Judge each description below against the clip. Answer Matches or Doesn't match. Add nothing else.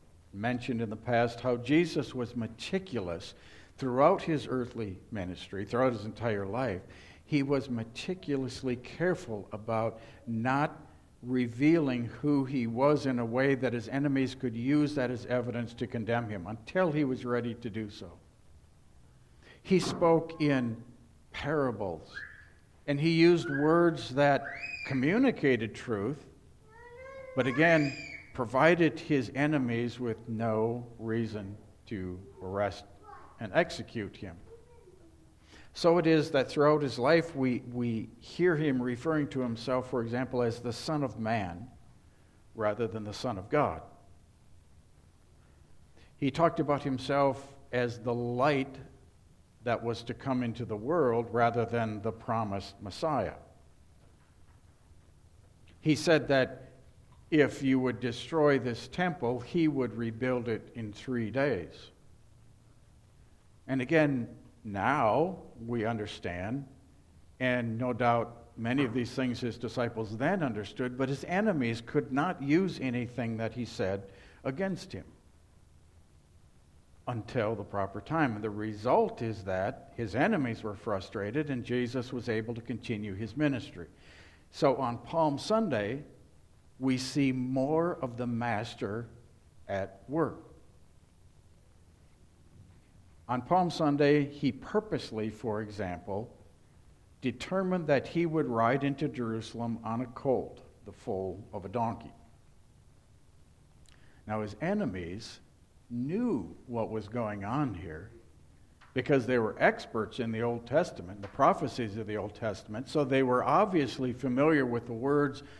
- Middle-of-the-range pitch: Doesn't match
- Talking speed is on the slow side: Matches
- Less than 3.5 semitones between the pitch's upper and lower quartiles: Doesn't match